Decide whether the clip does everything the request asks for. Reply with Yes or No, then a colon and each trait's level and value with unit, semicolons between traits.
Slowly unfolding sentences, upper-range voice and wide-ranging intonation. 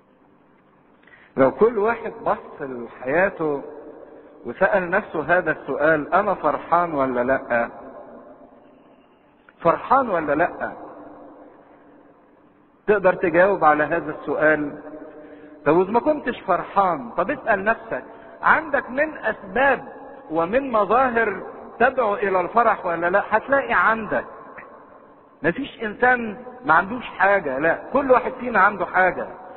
Yes: slow, 105 wpm; high, 205 Hz; wide, 6.7 semitones